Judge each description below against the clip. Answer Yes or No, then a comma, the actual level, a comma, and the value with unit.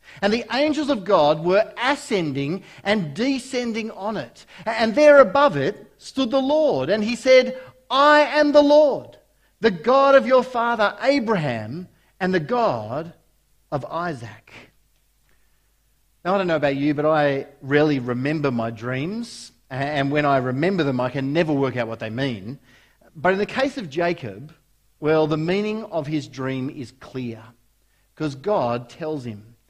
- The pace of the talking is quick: No, average, 160 wpm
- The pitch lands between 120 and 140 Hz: No, medium, 170 Hz